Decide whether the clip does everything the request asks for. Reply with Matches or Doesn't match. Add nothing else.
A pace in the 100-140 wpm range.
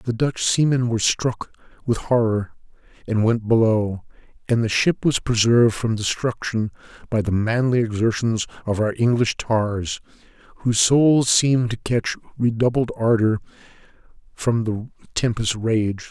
Matches